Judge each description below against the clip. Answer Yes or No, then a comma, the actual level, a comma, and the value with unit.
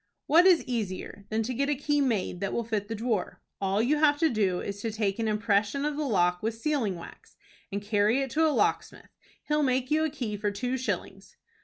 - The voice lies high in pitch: Yes, high, 230 Hz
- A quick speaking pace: Yes, fast, 225 wpm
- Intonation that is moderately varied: No, wide, 5.8 semitones